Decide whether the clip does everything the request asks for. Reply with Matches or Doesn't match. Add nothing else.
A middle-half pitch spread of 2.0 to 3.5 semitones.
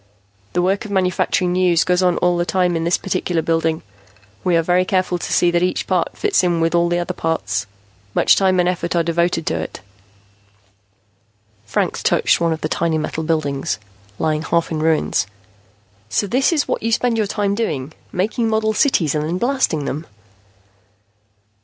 Matches